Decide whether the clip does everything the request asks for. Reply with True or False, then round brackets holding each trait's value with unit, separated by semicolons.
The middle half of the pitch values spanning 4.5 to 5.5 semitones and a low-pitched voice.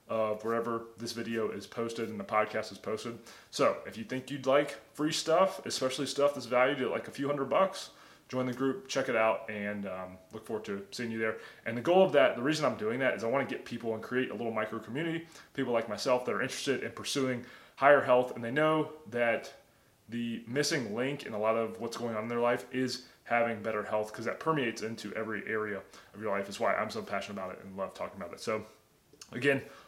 False (3.6 semitones; 120 Hz)